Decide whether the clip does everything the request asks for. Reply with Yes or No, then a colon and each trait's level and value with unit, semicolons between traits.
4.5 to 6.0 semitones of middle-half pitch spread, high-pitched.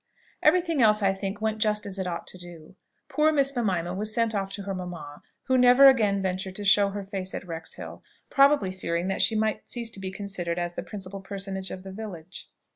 No: average, 2.9 semitones; high, 195 Hz